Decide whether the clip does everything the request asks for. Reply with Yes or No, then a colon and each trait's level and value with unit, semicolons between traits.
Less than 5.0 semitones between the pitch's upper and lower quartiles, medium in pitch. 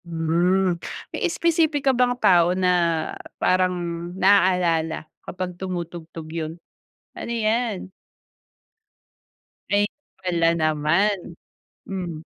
Yes: average, 3.3 semitones; medium, 180 Hz